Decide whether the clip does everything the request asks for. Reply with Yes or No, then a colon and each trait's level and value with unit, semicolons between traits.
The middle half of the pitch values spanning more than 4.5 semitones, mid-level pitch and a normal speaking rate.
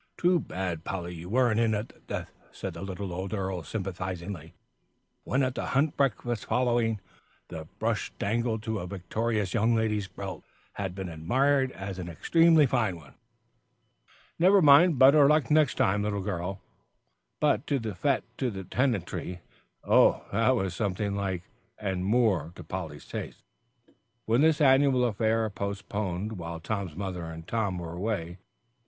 No: average, 4.9 semitones; low, 105 Hz; average, 160 wpm